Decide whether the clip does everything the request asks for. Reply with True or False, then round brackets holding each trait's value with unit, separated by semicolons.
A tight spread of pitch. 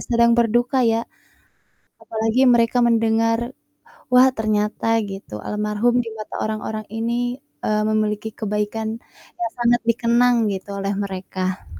True (2.1 semitones)